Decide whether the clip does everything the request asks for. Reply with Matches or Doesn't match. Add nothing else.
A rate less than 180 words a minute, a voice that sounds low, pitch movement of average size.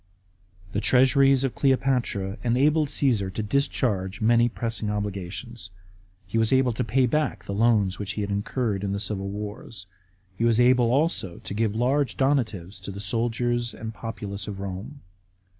Matches